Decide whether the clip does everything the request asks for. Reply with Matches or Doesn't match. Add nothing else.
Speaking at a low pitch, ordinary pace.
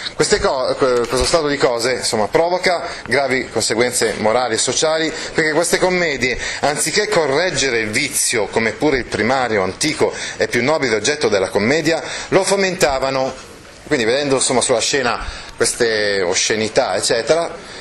Doesn't match